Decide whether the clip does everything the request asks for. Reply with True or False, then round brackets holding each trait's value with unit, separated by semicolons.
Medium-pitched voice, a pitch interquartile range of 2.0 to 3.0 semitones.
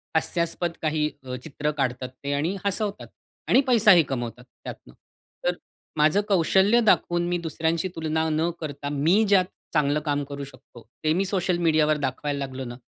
False (155 Hz; 3.7 semitones)